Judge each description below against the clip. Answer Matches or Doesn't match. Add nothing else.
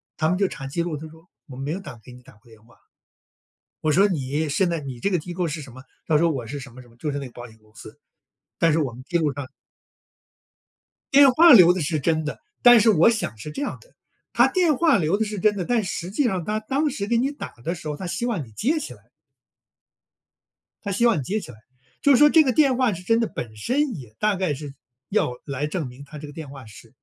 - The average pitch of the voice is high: Doesn't match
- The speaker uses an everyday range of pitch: Doesn't match